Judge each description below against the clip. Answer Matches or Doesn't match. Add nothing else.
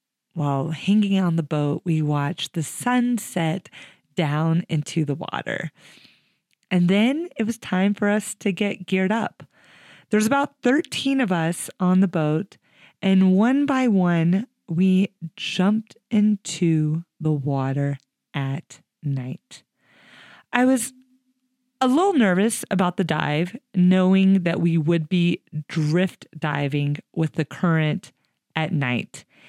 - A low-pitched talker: Doesn't match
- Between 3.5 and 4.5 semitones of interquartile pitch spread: Doesn't match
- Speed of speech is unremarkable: Doesn't match